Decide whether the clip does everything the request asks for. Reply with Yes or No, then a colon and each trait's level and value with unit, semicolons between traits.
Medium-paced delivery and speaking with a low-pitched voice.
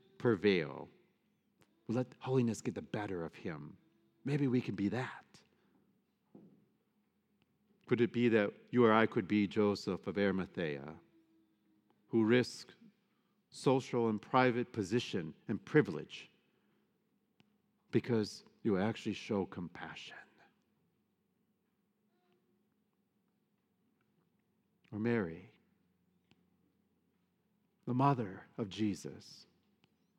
No: slow, 90 wpm; low, 130 Hz